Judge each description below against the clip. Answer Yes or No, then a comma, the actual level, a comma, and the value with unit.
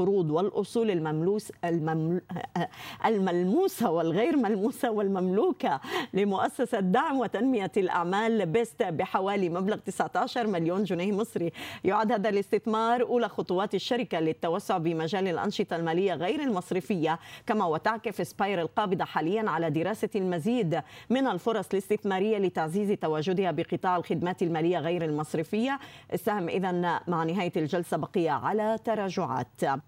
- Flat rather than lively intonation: No, average, 4.2 semitones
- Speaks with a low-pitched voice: No, high, 195 Hz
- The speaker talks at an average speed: Yes, average, 115 wpm